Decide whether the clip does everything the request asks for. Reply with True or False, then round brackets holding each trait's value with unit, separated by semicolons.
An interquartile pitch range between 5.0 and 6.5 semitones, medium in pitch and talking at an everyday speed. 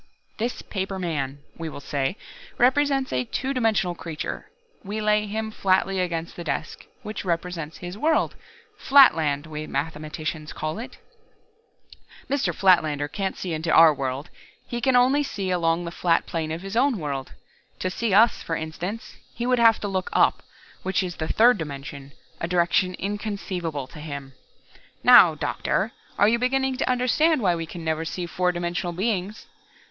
True (5.4 semitones; 180 Hz; 165 wpm)